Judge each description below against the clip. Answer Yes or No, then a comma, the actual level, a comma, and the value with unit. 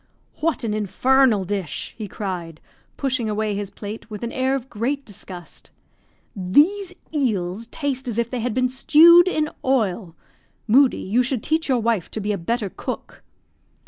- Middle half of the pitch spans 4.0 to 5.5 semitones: Yes, average, 4.6 semitones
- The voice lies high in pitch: Yes, high, 230 Hz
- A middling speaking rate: Yes, average, 165 wpm